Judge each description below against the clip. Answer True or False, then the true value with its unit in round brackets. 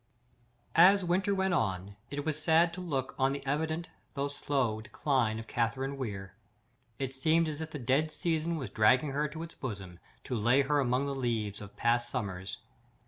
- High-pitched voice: False (135 Hz)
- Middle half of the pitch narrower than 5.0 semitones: False (5.3 semitones)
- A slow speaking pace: False (190 wpm)